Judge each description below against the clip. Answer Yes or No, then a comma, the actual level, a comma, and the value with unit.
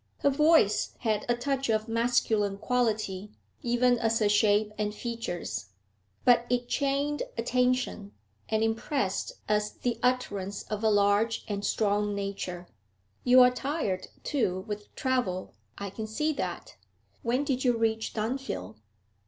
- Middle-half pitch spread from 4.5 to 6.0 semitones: No, average, 3.5 semitones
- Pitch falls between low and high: No, high, 225 Hz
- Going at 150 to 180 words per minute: No, slow, 135 wpm